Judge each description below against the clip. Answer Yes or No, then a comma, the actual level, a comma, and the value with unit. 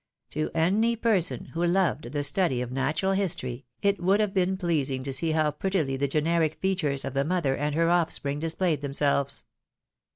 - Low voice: No, medium, 160 Hz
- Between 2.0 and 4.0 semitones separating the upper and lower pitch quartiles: No, average, 4.8 semitones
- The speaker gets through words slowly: No, average, 185 wpm